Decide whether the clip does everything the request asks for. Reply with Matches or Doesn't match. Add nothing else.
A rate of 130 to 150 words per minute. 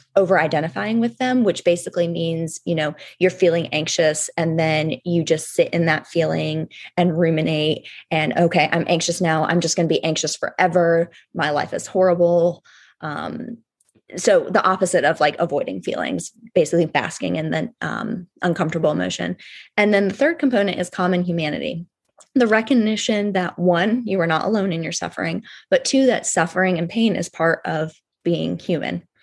Doesn't match